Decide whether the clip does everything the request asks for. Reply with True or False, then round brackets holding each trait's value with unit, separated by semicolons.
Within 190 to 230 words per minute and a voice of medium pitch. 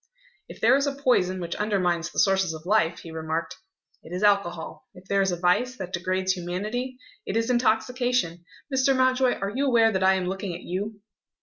False (200 wpm; 195 Hz)